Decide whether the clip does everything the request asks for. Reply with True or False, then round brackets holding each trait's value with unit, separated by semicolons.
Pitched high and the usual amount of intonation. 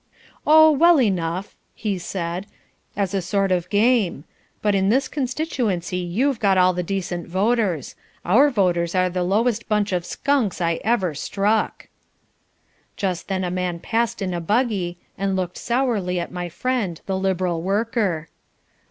True (195 Hz; 4.2 semitones)